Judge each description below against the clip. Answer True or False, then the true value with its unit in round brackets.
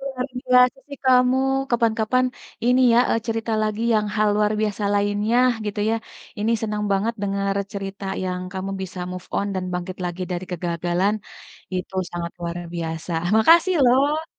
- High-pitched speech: True (210 Hz)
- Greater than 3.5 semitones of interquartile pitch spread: True (4.1 semitones)